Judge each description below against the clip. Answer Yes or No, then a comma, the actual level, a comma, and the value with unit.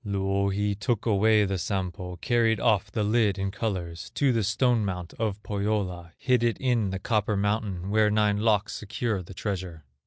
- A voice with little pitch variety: Yes, narrow, 2.3 semitones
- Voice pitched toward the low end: Yes, low, 105 Hz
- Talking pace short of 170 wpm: No, average, 175 wpm